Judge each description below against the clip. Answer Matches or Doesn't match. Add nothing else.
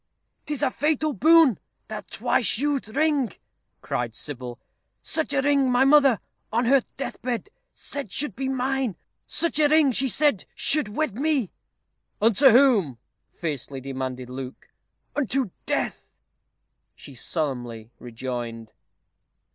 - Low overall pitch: Doesn't match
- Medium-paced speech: Doesn't match